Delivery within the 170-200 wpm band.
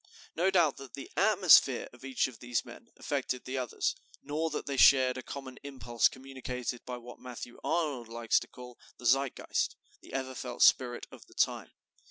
Yes: average, 185 wpm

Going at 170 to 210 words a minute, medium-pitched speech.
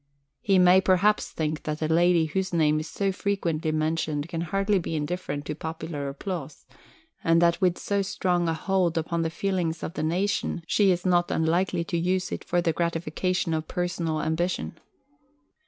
Yes: average, 175 wpm; medium, 170 Hz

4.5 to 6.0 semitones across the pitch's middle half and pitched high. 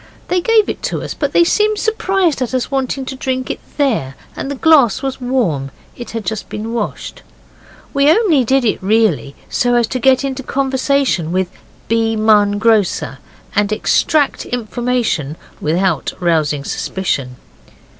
Yes: average, 5.2 semitones; high, 240 Hz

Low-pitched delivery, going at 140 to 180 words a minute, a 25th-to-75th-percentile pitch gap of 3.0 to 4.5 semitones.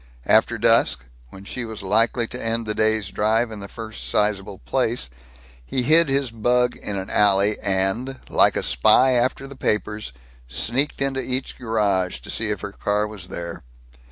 Yes: low, 110 Hz; average, 175 wpm; average, 3.7 semitones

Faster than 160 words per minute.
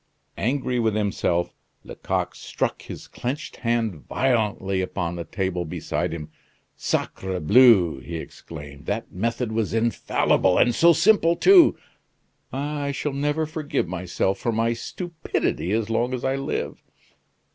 No: slow, 135 wpm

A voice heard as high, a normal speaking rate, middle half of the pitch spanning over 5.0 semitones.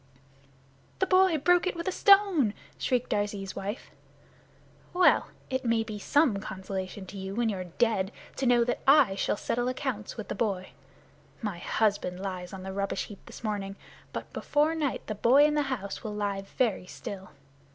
Yes: high, 215 Hz; average, 175 wpm; wide, 5.6 semitones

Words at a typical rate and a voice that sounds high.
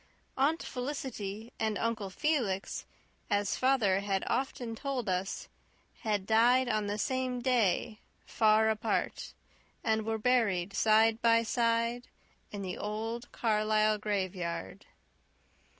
No: slow, 115 wpm; high, 220 Hz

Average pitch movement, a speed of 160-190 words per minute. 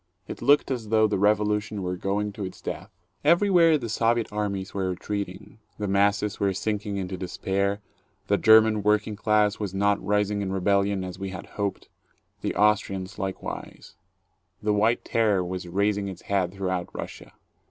No: narrow, 1.7 semitones; average, 165 wpm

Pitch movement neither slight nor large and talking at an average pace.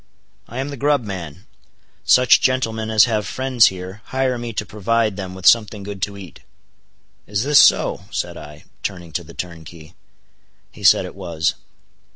Yes: average, 4.6 semitones; average, 170 wpm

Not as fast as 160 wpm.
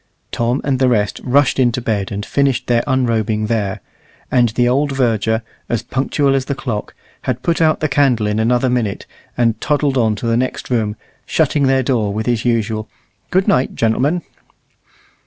No: average, 175 wpm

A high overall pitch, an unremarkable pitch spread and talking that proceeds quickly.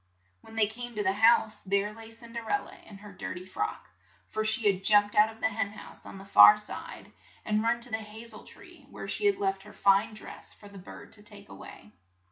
No: high, 215 Hz; narrow, 1.9 semitones; fast, 250 wpm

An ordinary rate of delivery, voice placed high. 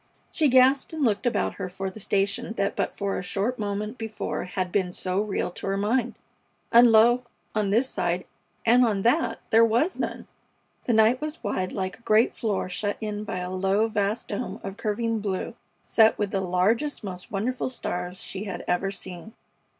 Yes: average, 190 wpm; high, 210 Hz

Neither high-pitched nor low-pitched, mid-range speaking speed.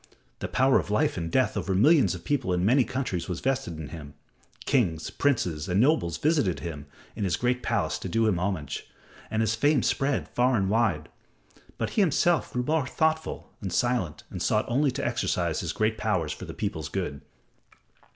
No: low, 110 Hz; average, 190 wpm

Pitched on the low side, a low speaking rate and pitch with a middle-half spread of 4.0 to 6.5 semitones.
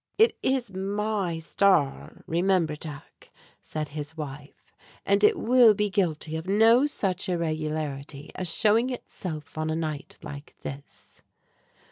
No: medium, 170 Hz; slow, 130 wpm; average, 5.2 semitones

